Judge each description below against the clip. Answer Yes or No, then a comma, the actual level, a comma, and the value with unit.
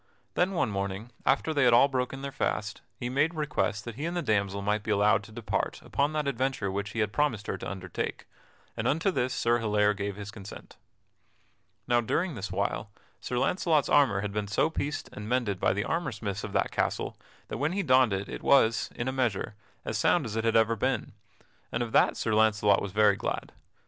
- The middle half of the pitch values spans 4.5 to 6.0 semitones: Yes, average, 4.8 semitones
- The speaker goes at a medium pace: No, fast, 215 wpm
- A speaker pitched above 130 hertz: No, low, 115 Hz